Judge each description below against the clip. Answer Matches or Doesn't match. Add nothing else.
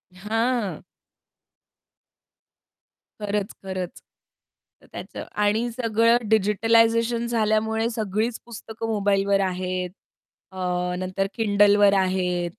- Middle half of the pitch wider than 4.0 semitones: Doesn't match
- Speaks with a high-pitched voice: Matches